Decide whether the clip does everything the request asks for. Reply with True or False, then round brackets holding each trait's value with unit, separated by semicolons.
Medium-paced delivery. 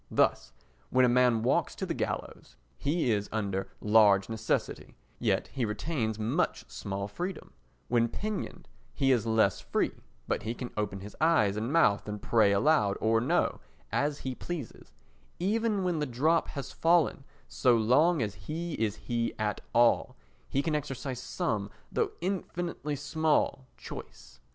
True (155 wpm)